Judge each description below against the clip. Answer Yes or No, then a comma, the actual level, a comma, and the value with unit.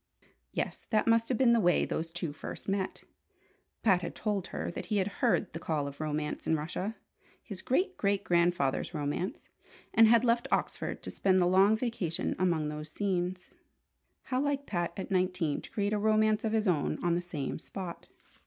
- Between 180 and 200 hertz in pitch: Yes, medium, 185 Hz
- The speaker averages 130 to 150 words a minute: No, average, 190 wpm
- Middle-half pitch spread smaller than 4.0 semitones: No, average, 4.4 semitones